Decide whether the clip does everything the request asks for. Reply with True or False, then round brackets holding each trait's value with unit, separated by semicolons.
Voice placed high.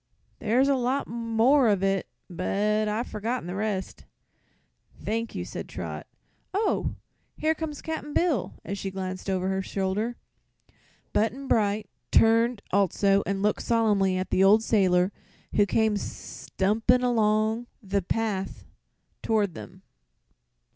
True (210 Hz)